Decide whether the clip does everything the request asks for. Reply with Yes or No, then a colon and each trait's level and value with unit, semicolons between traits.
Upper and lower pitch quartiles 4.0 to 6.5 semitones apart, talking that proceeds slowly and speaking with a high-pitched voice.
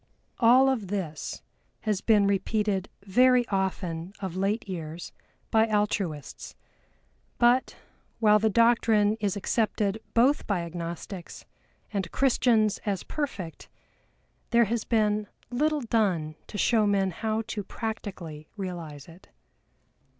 No: average, 3.5 semitones; slow, 115 wpm; high, 205 Hz